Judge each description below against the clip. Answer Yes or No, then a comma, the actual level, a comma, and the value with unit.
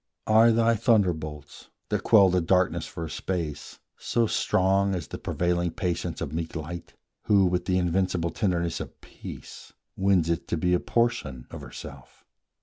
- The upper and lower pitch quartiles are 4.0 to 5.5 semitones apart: No, average, 2.9 semitones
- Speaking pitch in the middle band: No, very low, 90 Hz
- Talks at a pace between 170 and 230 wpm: No, average, 160 wpm